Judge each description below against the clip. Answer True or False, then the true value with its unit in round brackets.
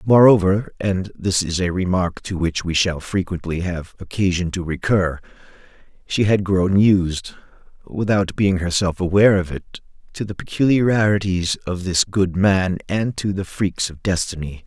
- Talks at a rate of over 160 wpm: False (145 wpm)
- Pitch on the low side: True (95 Hz)